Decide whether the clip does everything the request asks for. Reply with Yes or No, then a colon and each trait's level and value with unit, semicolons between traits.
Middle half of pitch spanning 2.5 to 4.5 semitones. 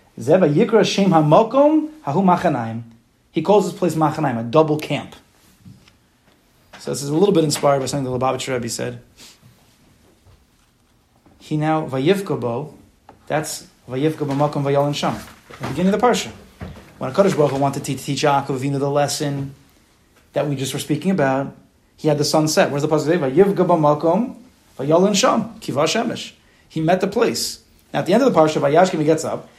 Yes: average, 4.2 semitones